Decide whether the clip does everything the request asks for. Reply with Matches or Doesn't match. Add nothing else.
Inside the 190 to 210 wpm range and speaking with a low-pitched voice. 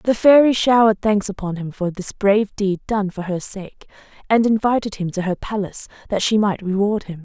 Doesn't match